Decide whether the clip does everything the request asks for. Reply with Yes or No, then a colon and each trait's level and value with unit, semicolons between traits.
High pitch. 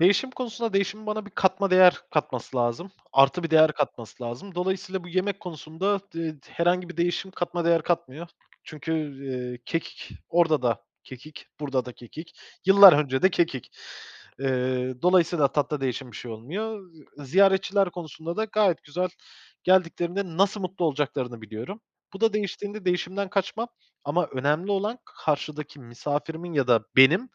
No: medium, 170 Hz